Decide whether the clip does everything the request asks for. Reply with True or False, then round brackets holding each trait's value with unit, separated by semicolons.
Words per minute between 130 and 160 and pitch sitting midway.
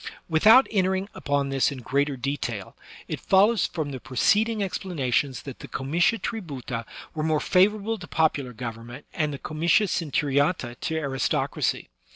True (145 wpm; 150 Hz)